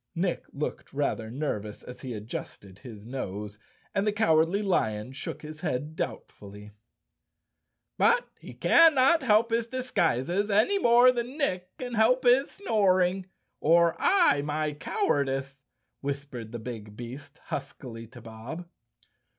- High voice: No, medium, 155 Hz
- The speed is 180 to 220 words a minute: No, slow, 135 wpm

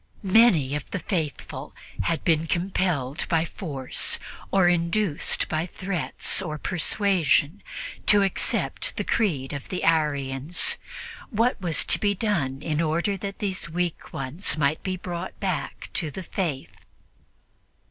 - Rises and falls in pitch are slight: No, average, 4.1 semitones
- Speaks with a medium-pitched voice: Yes, medium, 170 Hz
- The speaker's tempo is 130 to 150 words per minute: Yes, slow, 135 wpm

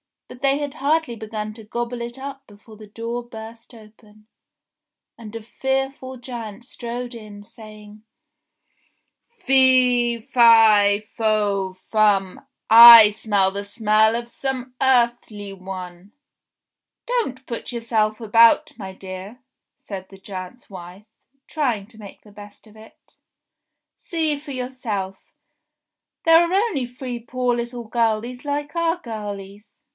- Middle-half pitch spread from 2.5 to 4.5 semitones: Yes, average, 3.2 semitones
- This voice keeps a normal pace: No, slow, 130 wpm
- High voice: Yes, high, 230 Hz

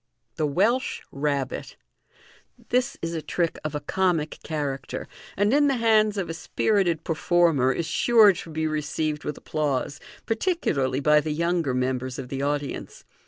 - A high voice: No, medium, 155 Hz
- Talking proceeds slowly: No, average, 160 wpm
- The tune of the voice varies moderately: Yes, average, 5.0 semitones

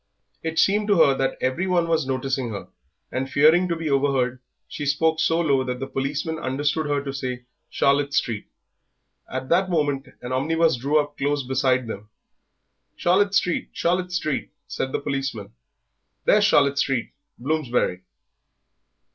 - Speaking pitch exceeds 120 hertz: Yes, medium, 140 Hz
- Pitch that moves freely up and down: No, average, 3.7 semitones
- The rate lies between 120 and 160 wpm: Yes, average, 155 wpm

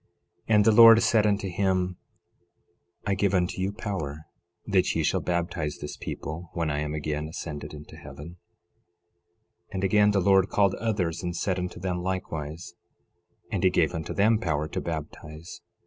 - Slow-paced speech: No, average, 170 wpm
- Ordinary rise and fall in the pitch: Yes, average, 4.0 semitones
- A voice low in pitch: Yes, very low, 90 Hz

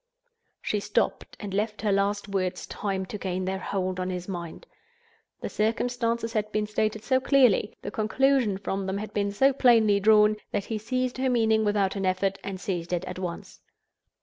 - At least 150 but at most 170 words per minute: No, average, 185 wpm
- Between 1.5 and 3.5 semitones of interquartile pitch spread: Yes, narrow, 2.6 semitones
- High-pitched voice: Yes, high, 205 Hz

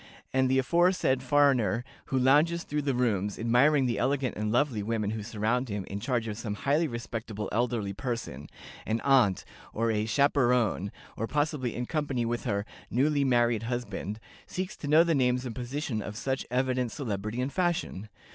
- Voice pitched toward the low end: Yes, low, 125 Hz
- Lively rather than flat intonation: No, average, 4.0 semitones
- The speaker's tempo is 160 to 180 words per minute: Yes, average, 175 wpm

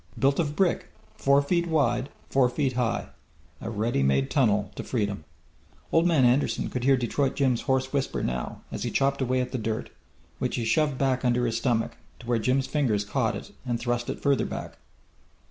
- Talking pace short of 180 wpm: No, average, 195 wpm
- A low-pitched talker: Yes, low, 125 Hz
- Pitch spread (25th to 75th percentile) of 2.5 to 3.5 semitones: Yes, average, 3.1 semitones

